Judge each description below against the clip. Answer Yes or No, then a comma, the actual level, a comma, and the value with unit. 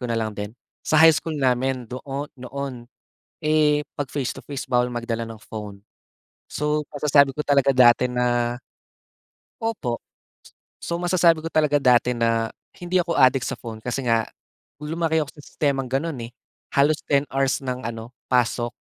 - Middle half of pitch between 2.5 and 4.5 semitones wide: Yes, average, 3.9 semitones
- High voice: No, low, 135 Hz